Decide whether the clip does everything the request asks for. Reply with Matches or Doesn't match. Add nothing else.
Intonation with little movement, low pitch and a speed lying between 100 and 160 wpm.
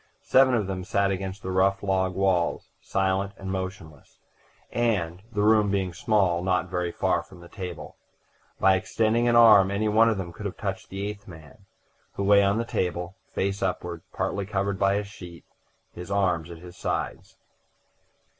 Doesn't match